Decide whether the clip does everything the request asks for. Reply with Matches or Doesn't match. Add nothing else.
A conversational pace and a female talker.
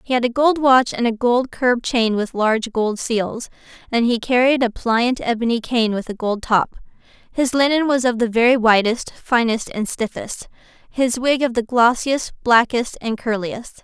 Matches